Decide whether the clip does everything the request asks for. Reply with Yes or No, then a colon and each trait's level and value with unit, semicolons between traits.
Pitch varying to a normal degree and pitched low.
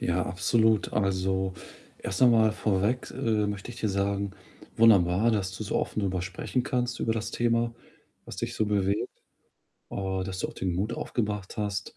Yes: average, 3.0 semitones; low, 105 Hz